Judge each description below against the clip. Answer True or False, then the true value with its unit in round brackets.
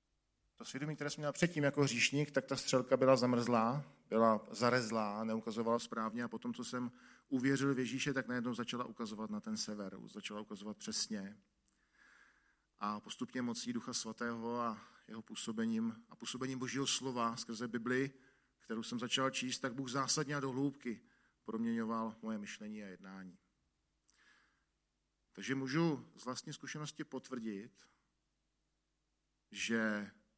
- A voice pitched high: False (125 Hz)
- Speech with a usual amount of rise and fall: True (3.4 semitones)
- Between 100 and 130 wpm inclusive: False (140 wpm)